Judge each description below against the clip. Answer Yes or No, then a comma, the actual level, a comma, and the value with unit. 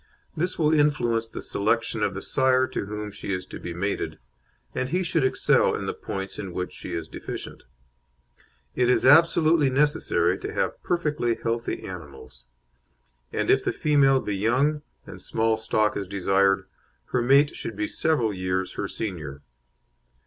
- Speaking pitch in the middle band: No, low, 115 Hz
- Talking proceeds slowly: No, average, 165 wpm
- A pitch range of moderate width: No, wide, 6.3 semitones